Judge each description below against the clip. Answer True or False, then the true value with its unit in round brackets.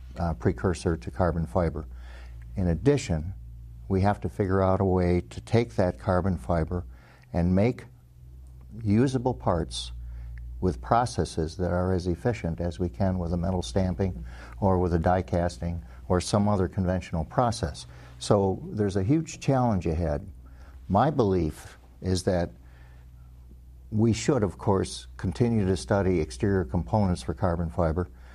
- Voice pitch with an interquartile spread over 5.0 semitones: True (5.4 semitones)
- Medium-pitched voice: False (90 Hz)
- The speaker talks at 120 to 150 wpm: True (145 wpm)